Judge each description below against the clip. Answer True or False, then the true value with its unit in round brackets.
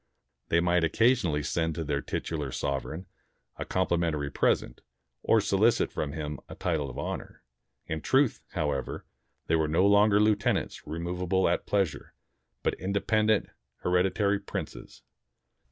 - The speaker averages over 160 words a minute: False (135 wpm)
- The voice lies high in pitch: False (85 Hz)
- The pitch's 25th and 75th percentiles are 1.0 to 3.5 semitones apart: False (4.7 semitones)